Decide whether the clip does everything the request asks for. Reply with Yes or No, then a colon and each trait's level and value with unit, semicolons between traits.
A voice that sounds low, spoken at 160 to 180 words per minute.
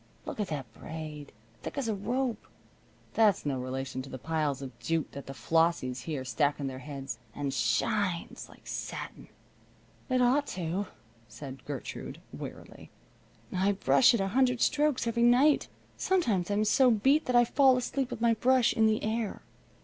No: high, 195 Hz; average, 170 wpm